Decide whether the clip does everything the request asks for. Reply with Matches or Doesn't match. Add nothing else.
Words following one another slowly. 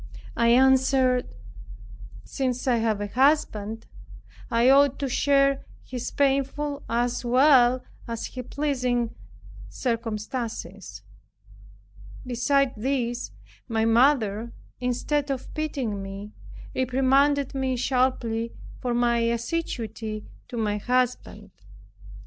Matches